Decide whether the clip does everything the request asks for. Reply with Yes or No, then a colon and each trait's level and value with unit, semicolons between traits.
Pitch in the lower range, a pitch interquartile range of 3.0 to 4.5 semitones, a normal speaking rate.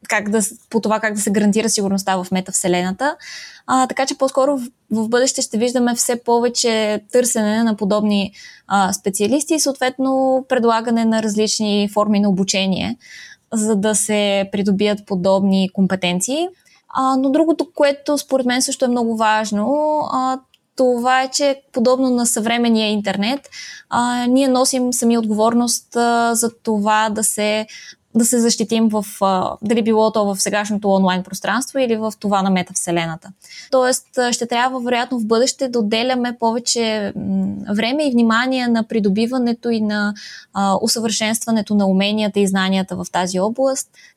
No: high, 225 Hz; average, 3.4 semitones; average, 150 wpm